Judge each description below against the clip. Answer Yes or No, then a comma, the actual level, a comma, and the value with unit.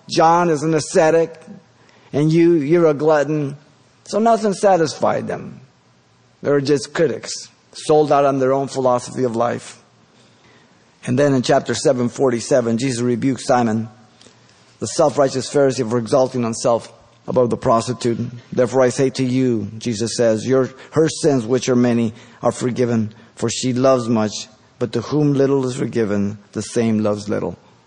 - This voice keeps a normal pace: Yes, average, 155 wpm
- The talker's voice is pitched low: Yes, low, 125 Hz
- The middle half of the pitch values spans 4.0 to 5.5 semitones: No, average, 3.6 semitones